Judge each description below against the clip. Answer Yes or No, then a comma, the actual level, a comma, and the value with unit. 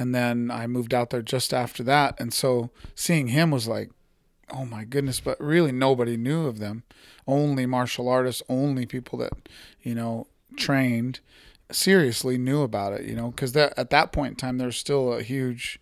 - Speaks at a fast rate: No, average, 190 wpm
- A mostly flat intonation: Yes, narrow, 2.3 semitones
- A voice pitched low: Yes, low, 125 Hz